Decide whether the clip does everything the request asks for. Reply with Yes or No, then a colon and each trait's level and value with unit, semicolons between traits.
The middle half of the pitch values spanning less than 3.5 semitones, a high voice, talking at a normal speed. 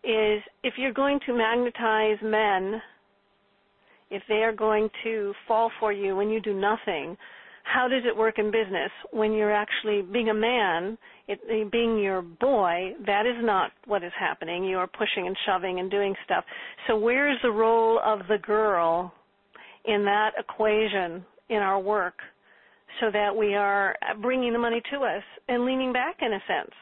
Yes: narrow, 2.5 semitones; high, 215 Hz; average, 175 wpm